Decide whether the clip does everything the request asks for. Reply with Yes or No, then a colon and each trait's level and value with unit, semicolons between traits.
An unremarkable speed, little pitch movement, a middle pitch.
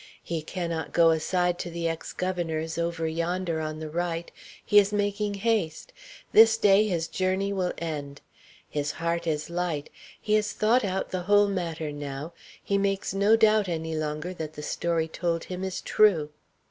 No: average, 170 wpm; average, 3.6 semitones; medium, 170 Hz